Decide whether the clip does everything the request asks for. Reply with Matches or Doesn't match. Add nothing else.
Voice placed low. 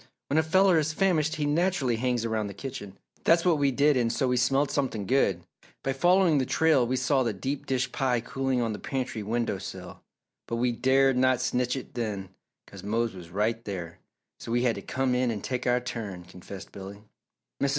Matches